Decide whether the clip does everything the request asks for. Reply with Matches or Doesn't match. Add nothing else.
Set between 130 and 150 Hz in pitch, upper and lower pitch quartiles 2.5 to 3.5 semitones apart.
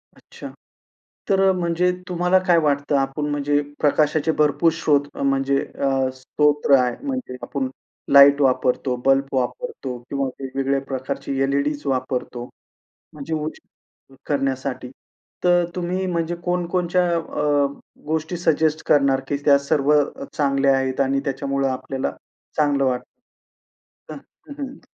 Matches